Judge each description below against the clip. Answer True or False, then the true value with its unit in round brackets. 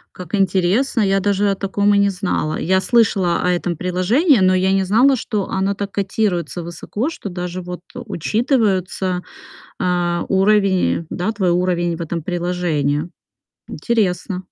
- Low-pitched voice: False (190 Hz)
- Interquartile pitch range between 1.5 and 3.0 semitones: True (2.5 semitones)